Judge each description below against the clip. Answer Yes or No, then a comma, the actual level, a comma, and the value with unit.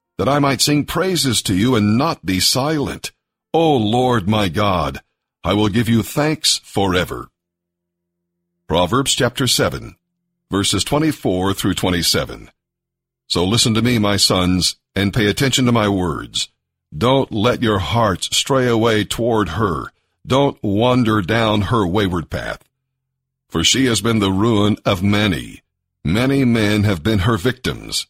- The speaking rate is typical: Yes, average, 145 wpm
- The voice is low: Yes, low, 110 Hz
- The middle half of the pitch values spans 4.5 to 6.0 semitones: Yes, average, 4.8 semitones